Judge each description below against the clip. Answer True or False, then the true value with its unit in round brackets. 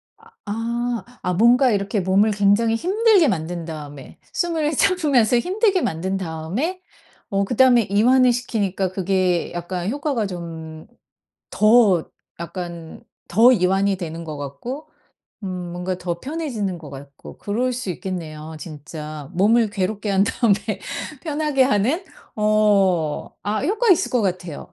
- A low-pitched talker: False (200 Hz)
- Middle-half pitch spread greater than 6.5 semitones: False (6.1 semitones)